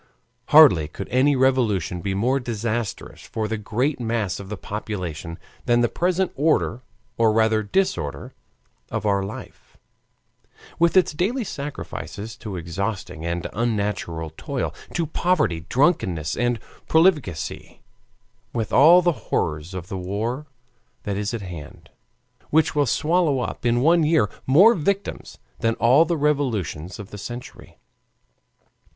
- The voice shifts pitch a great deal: Yes, wide, 7.2 semitones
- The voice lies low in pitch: Yes, low, 115 Hz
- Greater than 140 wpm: No, slow, 135 wpm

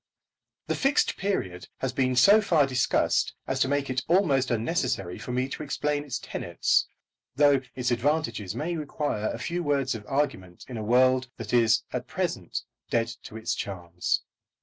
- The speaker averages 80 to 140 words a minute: No, average, 170 wpm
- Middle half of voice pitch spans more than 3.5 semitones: Yes, average, 4.4 semitones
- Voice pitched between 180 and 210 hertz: No, low, 130 Hz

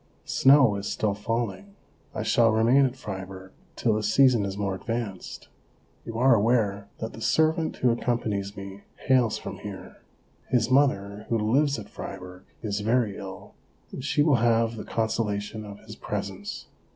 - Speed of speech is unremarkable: Yes, average, 165 wpm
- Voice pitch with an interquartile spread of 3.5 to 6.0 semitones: No, average, 3.1 semitones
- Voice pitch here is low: Yes, low, 110 Hz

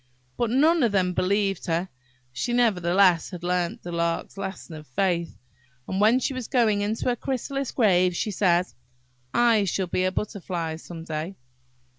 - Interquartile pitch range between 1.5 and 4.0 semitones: No, average, 4.4 semitones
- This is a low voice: No, high, 190 Hz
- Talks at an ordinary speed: Yes, average, 160 wpm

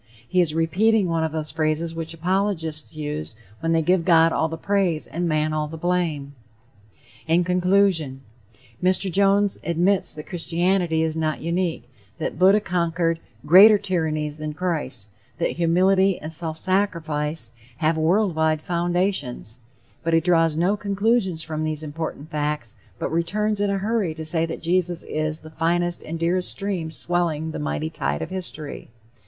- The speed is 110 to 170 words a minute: Yes, average, 160 wpm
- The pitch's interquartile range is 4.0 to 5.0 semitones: No, average, 2.8 semitones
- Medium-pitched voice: Yes, medium, 165 Hz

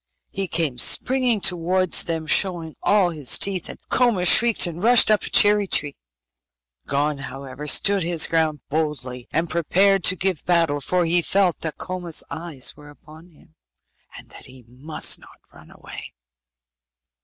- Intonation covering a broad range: No, average, 4.0 semitones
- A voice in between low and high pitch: Yes, medium, 170 Hz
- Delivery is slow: No, average, 155 wpm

